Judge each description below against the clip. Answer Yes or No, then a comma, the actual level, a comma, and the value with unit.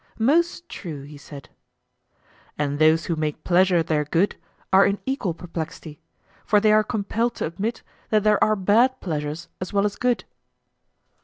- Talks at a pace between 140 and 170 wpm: Yes, average, 160 wpm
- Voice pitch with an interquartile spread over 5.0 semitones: Yes, wide, 5.4 semitones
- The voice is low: No, high, 190 Hz